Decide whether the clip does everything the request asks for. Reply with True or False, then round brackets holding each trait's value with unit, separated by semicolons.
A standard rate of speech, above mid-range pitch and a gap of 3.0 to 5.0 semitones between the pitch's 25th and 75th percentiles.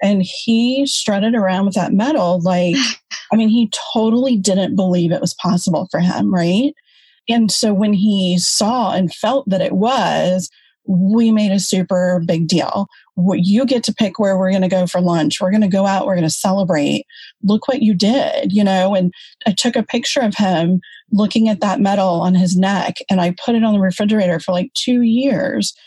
True (195 wpm; 195 Hz; 3.6 semitones)